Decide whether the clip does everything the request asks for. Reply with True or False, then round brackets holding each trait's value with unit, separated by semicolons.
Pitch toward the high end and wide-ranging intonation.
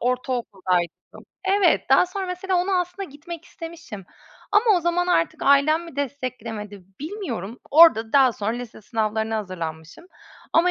True (280 Hz; 8.2 semitones)